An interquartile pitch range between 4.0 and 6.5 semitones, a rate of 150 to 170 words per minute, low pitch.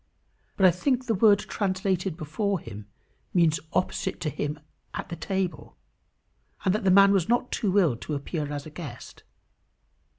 No: average, 4.4 semitones; average, 165 wpm; medium, 180 Hz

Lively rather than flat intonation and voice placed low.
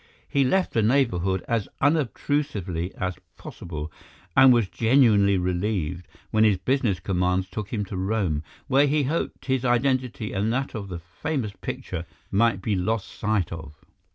Yes: wide, 5.7 semitones; low, 105 Hz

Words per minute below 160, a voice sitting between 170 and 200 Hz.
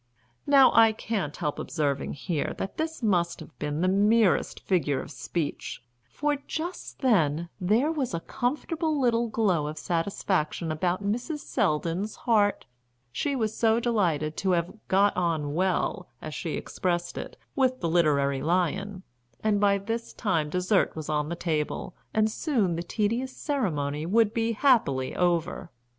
Yes: average, 150 wpm; high, 190 Hz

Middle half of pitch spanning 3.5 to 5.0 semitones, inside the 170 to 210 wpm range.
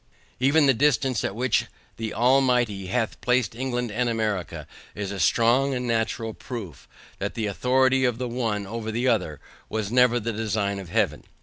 No: average, 2.9 semitones; average, 175 wpm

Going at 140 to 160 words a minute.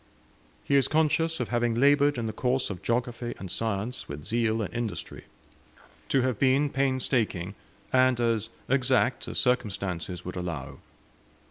Yes: average, 145 wpm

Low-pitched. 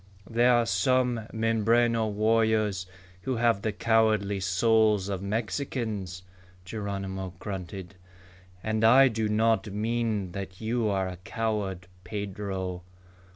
Yes: low, 110 Hz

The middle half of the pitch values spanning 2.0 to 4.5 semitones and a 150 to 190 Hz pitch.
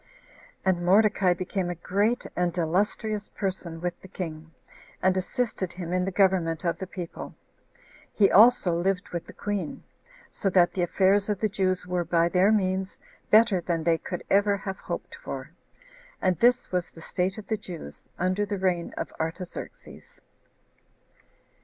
Yes: narrow, 2.4 semitones; medium, 185 Hz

